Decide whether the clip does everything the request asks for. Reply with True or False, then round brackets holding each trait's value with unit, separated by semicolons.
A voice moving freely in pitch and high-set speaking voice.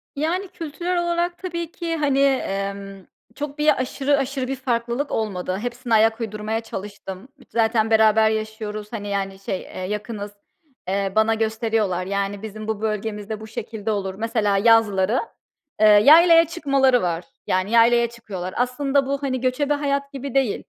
False (4.9 semitones; 225 Hz)